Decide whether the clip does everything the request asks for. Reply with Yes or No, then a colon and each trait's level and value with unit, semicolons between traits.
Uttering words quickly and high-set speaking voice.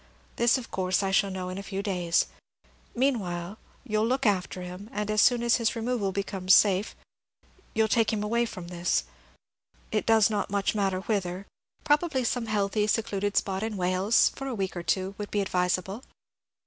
No: average, 185 wpm; high, 205 Hz